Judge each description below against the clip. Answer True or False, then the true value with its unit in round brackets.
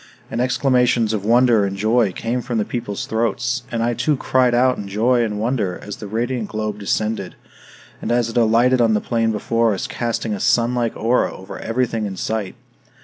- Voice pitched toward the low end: True (115 Hz)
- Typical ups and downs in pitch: False (2.3 semitones)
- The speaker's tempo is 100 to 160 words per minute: False (195 wpm)